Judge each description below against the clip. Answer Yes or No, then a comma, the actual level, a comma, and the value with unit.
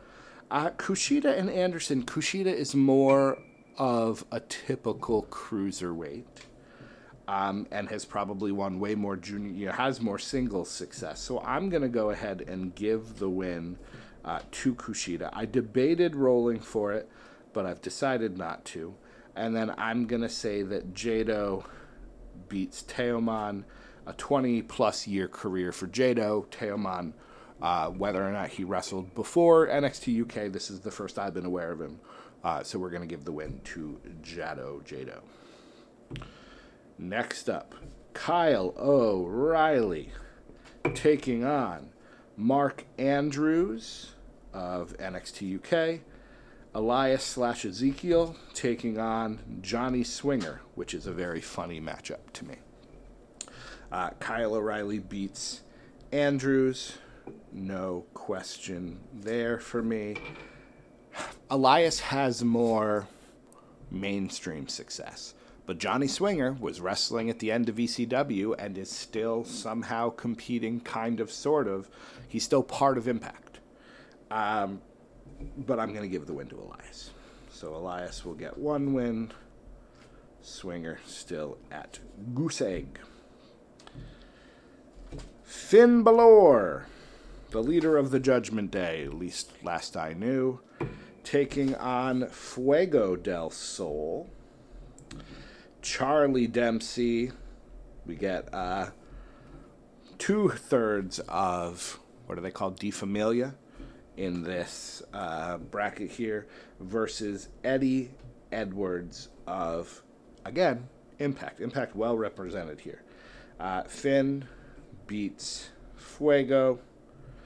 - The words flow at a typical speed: No, slow, 120 wpm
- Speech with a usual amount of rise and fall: Yes, average, 4.9 semitones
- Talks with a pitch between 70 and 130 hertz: Yes, low, 115 Hz